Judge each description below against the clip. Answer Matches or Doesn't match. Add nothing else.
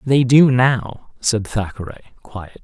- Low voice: Matches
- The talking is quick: Doesn't match